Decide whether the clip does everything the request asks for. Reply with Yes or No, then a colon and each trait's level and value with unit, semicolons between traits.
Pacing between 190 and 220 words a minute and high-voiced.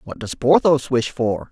No: average, 200 wpm; low, 130 Hz